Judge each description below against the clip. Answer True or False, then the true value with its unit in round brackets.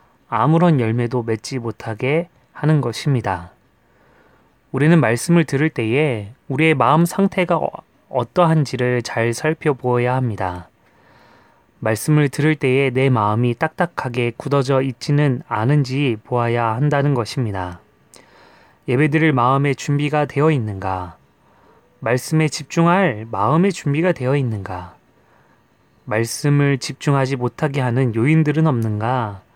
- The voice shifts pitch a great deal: False (4.5 semitones)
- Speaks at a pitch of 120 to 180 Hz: True (135 Hz)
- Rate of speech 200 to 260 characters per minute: False (275 characters per minute)